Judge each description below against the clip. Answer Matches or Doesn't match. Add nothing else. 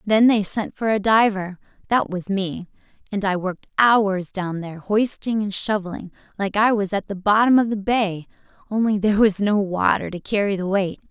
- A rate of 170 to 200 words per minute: Matches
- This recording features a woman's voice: Matches